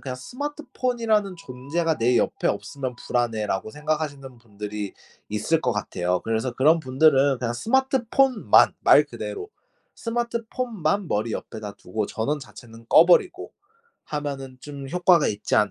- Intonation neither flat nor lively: No, wide, 8.8 semitones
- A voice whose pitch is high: No, medium, 140 Hz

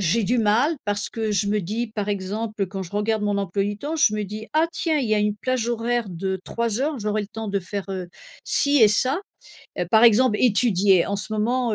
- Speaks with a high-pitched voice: Yes, high, 215 Hz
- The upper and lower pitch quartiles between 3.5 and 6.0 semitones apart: No, average, 2.8 semitones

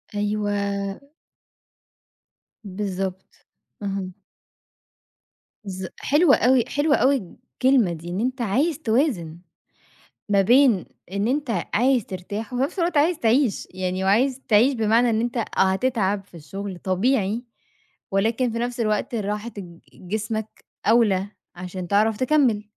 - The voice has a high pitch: Yes, high, 215 Hz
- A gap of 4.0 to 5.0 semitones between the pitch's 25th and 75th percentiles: Yes, average, 4.4 semitones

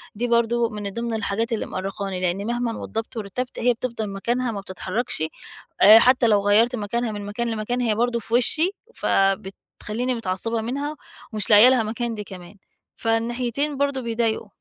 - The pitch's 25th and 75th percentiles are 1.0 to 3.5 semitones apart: Yes, average, 2.8 semitones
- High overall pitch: Yes, high, 225 Hz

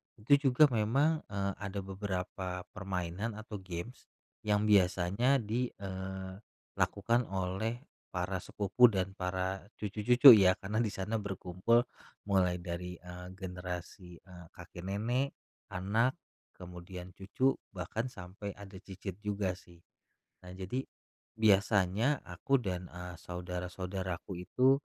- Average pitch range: Yes, average, 3.0 semitones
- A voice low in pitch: Yes, very low, 95 Hz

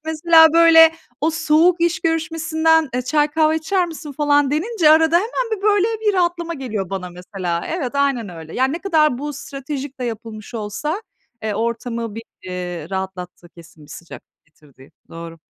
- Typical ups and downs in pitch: No, wide, 8.0 semitones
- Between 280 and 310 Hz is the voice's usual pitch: Yes, very high, 290 Hz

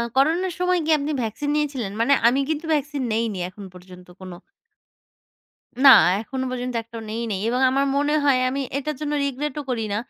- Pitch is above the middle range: Yes, very high, 265 Hz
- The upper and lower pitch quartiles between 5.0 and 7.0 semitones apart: No, average, 4.5 semitones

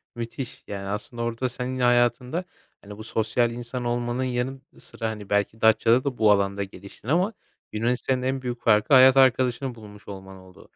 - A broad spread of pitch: No, average, 3.3 semitones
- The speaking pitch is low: Yes, low, 120 Hz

